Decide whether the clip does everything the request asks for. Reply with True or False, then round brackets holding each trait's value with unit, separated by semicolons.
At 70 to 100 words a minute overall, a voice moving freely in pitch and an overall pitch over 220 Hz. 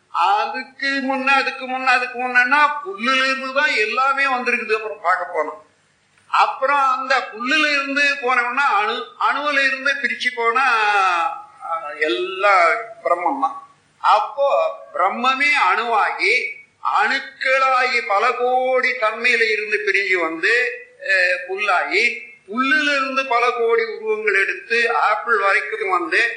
True (80 wpm; 8.2 semitones; 270 Hz)